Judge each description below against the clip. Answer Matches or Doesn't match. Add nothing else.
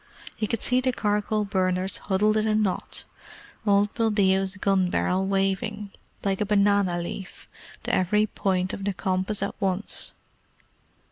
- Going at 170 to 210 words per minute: Doesn't match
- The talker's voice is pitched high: Matches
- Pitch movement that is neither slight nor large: Doesn't match